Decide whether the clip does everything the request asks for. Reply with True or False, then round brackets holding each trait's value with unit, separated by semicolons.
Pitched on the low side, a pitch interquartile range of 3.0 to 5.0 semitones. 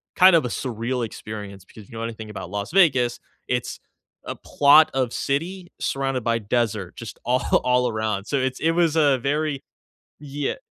True (125 Hz; 4.5 semitones)